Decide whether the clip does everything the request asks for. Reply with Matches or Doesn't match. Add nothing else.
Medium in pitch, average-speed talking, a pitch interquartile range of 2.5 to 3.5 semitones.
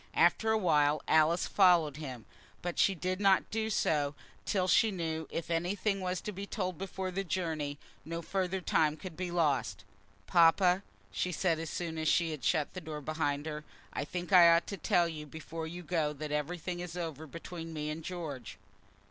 Matches